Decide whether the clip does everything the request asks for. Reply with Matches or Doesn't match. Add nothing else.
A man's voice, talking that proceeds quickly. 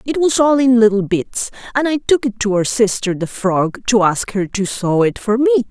Doesn't match